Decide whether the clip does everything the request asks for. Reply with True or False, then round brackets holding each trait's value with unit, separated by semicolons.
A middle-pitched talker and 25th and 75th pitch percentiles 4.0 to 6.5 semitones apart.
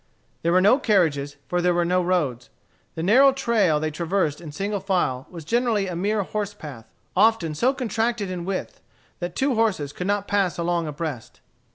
True (180 Hz; 4.5 semitones)